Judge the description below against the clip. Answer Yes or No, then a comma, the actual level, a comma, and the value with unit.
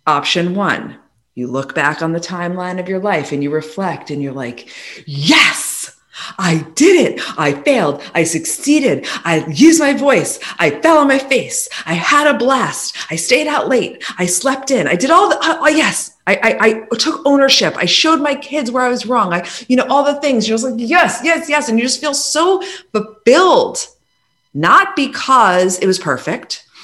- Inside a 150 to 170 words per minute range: No, average, 195 wpm